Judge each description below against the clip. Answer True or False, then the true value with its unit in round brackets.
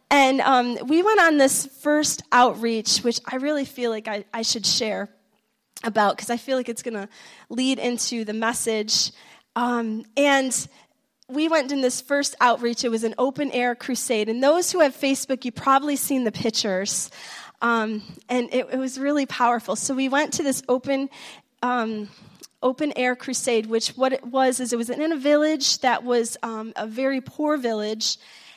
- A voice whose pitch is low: False (250 Hz)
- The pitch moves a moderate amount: True (3.0 semitones)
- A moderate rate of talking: True (180 wpm)